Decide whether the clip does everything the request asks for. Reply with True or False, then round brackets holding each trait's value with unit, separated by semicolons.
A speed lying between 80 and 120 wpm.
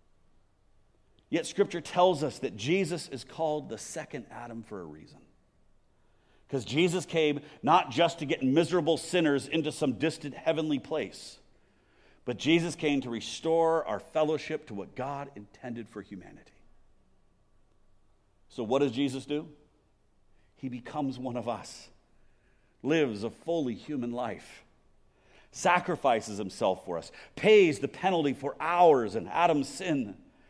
False (135 wpm)